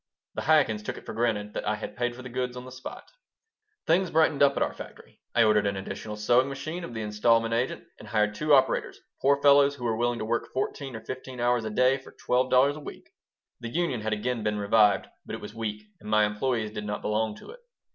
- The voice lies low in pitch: Yes, low, 120 Hz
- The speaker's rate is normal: No, fast, 240 wpm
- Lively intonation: No, average, 3.6 semitones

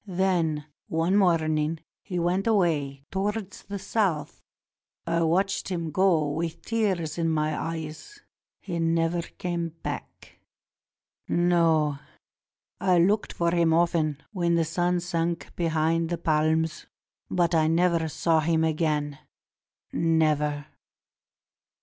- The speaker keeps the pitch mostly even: Yes, narrow, 2.0 semitones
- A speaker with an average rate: No, slow, 120 wpm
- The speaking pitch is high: No, medium, 165 Hz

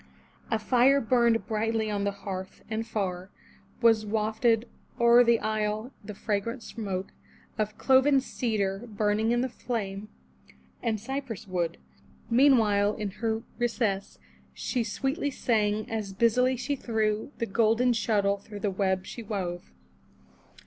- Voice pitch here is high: Yes, high, 220 Hz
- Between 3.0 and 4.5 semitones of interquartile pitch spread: No, narrow, 2.6 semitones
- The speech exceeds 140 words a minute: No, slow, 135 wpm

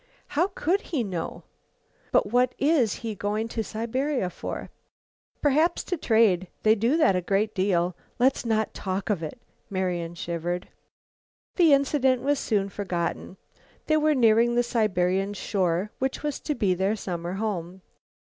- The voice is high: Yes, high, 215 Hz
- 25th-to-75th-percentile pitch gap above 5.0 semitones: Yes, wide, 5.6 semitones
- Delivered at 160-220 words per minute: No, average, 150 wpm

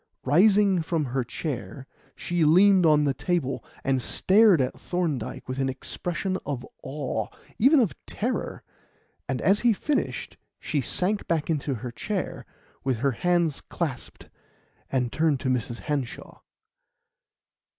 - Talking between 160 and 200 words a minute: No, slow, 135 wpm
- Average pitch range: No, wide, 5.8 semitones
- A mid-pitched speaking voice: Yes, medium, 150 Hz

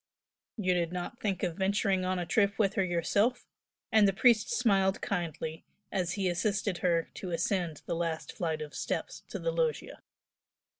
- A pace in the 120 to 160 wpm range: No, average, 170 wpm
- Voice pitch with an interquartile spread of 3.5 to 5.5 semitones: No, average, 2.9 semitones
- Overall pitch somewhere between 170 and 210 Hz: Yes, medium, 185 Hz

